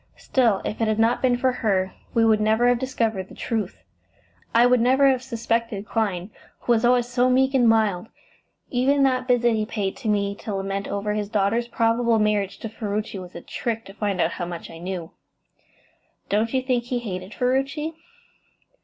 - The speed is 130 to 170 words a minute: No, average, 190 wpm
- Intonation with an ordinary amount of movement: Yes, average, 3.4 semitones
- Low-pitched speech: No, high, 225 Hz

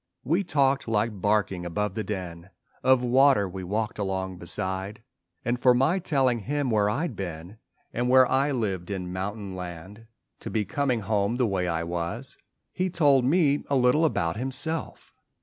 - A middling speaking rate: Yes, average, 165 wpm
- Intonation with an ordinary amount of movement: No, wide, 5.8 semitones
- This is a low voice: Yes, low, 110 Hz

